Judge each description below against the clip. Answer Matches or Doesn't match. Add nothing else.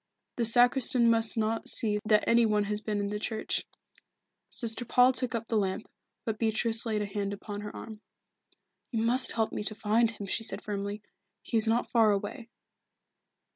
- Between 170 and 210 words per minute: Matches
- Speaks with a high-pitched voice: Matches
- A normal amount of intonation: Doesn't match